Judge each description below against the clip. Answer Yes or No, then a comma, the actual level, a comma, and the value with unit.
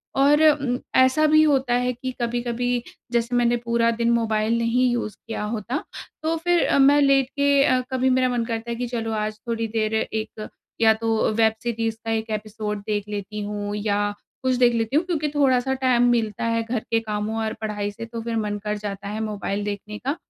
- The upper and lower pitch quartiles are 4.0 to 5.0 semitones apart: No, average, 2.8 semitones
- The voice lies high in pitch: Yes, high, 230 Hz